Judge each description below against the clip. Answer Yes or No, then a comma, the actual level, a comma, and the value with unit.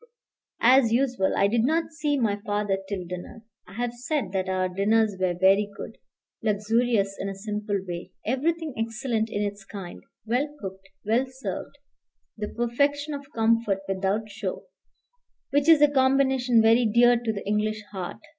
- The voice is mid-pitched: No, high, 220 Hz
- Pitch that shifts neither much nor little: Yes, average, 4.1 semitones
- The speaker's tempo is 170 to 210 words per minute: No, average, 160 wpm